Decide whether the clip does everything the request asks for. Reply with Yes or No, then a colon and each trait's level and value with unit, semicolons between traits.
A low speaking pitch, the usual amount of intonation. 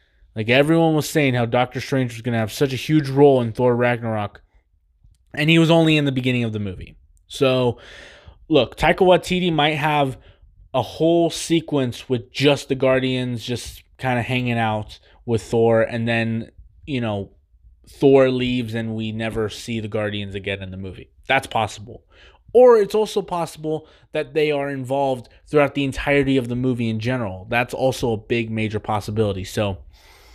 Yes: low, 120 Hz; average, 4.6 semitones